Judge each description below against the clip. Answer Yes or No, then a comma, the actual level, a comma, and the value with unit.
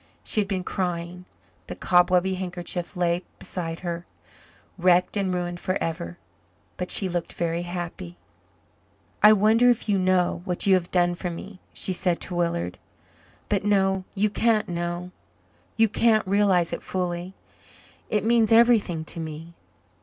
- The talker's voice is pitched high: No, medium, 180 Hz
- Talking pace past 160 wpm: No, average, 145 wpm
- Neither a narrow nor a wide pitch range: No, narrow, 2.3 semitones